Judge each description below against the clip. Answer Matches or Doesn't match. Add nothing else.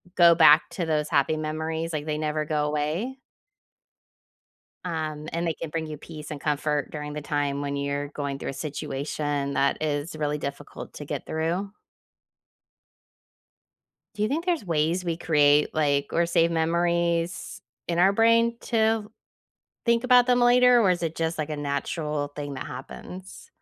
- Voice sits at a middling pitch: Matches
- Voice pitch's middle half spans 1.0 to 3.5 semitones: Matches